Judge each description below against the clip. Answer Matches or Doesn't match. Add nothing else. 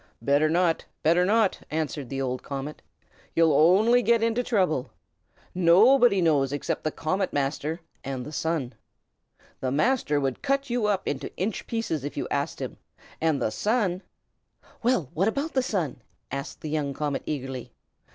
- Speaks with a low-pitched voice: Doesn't match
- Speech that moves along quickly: Doesn't match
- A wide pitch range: Matches